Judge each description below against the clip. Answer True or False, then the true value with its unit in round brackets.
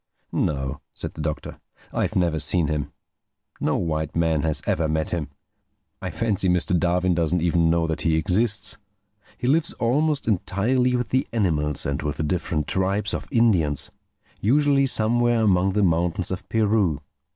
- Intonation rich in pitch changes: True (5.9 semitones)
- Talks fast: False (155 wpm)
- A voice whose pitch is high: False (90 Hz)